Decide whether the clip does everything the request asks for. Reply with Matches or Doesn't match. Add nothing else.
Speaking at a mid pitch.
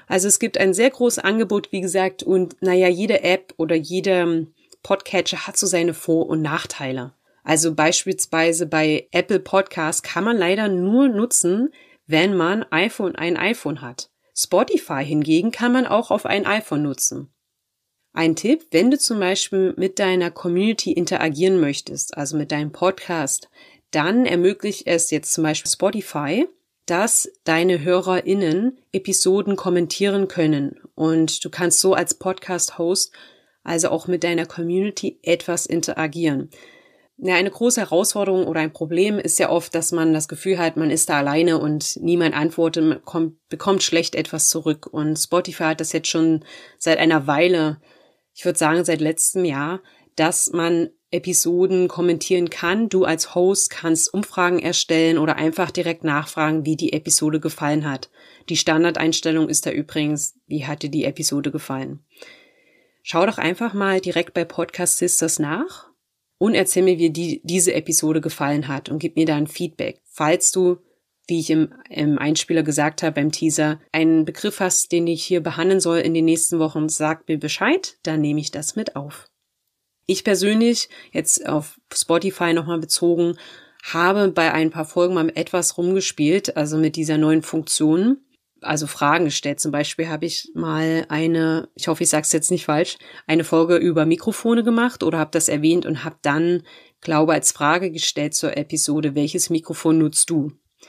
Matches